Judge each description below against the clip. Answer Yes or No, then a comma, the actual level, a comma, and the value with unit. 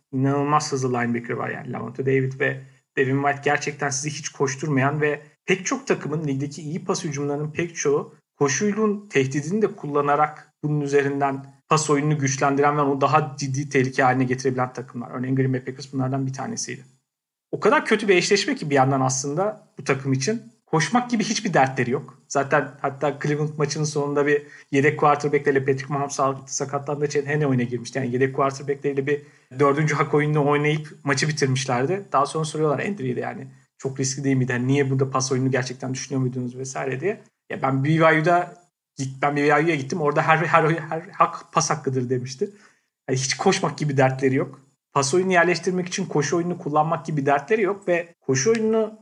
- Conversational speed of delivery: No, fast, 175 wpm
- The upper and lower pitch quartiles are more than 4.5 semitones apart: No, average, 2.8 semitones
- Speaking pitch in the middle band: Yes, medium, 145 Hz